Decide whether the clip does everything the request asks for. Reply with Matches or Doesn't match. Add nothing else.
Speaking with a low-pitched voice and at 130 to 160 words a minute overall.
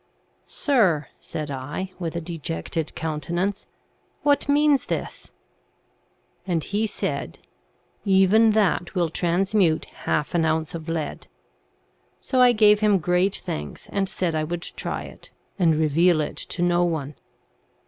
Doesn't match